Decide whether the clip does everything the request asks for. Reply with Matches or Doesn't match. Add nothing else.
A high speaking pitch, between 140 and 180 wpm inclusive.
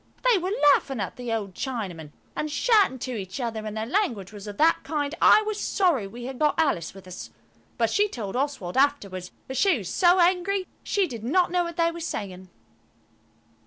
Doesn't match